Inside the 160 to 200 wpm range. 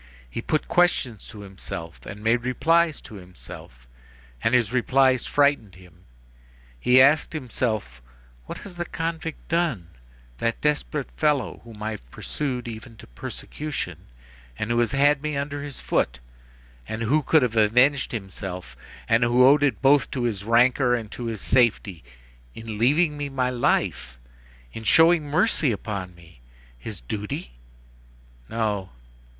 No: average, 145 wpm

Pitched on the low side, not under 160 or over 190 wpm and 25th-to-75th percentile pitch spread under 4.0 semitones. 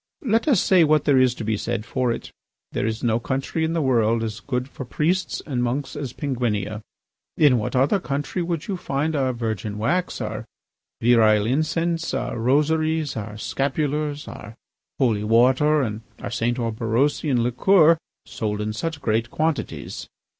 No: low, 130 Hz; average, 165 wpm; average, 5.2 semitones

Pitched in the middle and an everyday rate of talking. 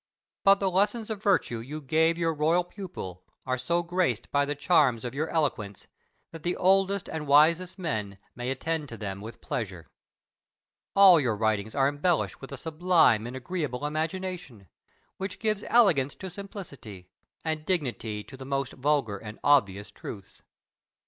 Yes: medium, 150 Hz; average, 160 wpm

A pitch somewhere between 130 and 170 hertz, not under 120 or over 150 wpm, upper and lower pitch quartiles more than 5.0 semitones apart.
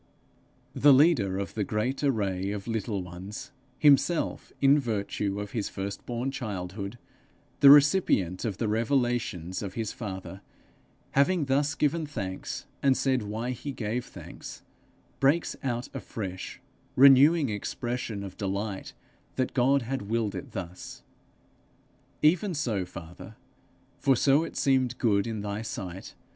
No: low, 115 Hz; slow, 135 wpm; wide, 5.5 semitones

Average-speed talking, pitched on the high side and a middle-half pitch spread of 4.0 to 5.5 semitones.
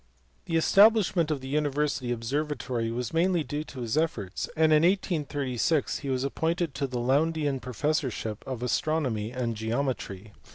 No: average, 150 wpm; medium, 140 Hz; average, 4.4 semitones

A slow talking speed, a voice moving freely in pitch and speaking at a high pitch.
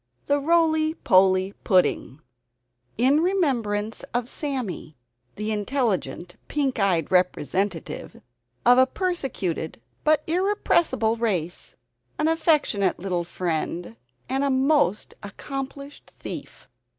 Yes: slow, 95 wpm; wide, 7.8 semitones; high, 235 Hz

